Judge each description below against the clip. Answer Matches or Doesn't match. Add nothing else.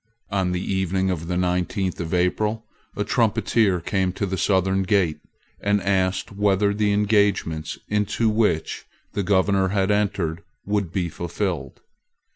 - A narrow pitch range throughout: Matches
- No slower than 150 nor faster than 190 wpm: Doesn't match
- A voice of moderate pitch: Doesn't match